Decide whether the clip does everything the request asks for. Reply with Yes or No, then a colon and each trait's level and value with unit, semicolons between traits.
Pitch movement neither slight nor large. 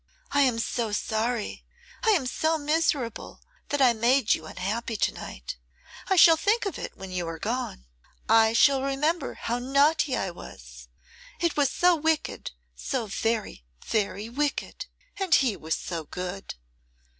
No: wide, 6.4 semitones